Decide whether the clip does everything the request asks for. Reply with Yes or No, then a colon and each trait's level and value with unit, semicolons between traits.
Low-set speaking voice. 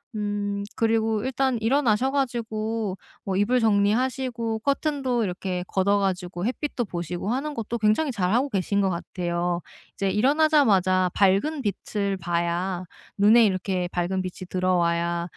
No: high, 205 Hz